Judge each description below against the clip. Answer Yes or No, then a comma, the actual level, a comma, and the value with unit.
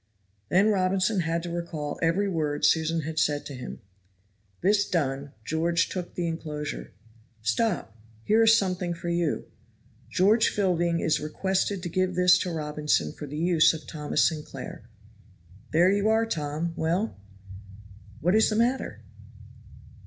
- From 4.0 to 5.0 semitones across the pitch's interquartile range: No, average, 3.6 semitones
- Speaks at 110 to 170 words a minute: Yes, average, 145 wpm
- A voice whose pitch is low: No, medium, 170 Hz